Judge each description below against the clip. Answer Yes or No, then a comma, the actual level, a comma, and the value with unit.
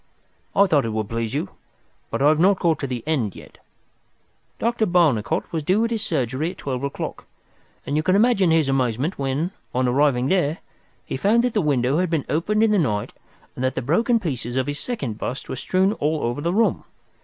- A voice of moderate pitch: Yes, medium, 150 Hz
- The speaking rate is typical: No, fast, 210 wpm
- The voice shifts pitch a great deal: Yes, wide, 6.3 semitones